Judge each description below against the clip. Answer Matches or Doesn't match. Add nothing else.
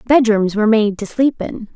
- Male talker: Doesn't match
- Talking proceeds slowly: Doesn't match